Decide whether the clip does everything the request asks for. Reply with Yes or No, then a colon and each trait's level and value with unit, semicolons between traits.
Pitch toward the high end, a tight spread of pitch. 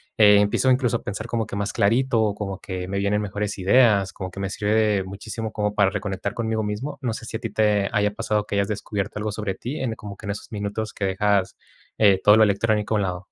No: low, 105 Hz; narrow, 1.8 semitones